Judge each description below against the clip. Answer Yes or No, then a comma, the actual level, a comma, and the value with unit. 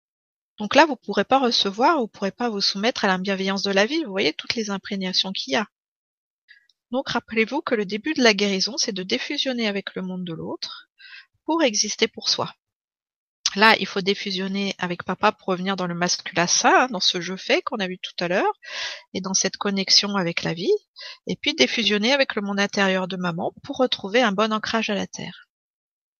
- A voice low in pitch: No, high, 210 Hz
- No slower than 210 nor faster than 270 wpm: Yes, average, 215 wpm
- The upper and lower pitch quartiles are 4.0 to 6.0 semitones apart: Yes, average, 4.4 semitones